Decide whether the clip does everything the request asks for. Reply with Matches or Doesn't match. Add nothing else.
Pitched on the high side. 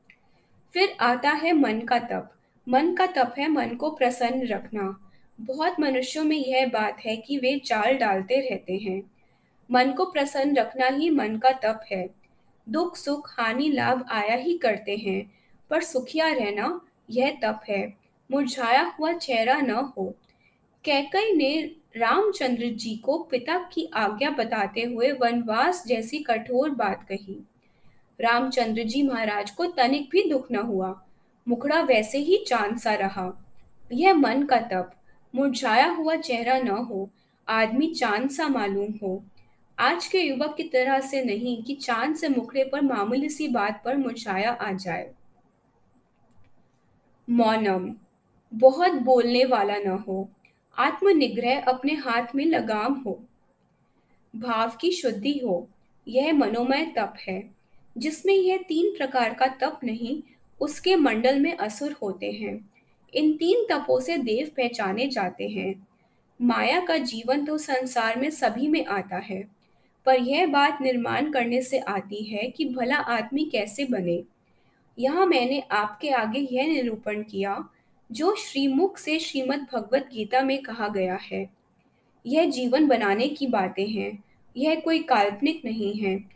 Matches